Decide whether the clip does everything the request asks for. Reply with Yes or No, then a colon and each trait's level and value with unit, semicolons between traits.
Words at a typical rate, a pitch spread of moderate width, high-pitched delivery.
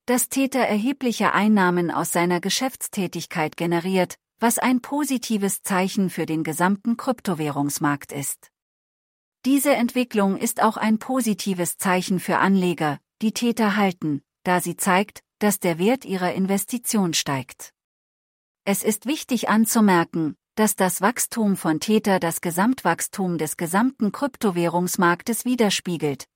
No: slow, 120 wpm; average, 4.6 semitones; high, 195 Hz